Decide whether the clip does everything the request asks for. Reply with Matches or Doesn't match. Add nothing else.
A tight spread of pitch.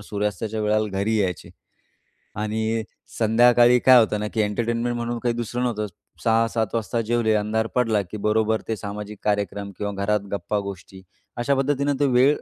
Matches